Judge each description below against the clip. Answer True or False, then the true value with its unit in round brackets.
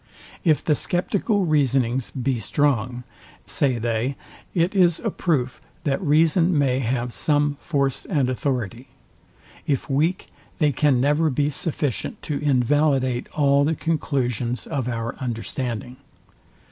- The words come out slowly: True (125 wpm)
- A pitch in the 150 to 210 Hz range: False (140 Hz)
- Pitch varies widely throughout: False (3.5 semitones)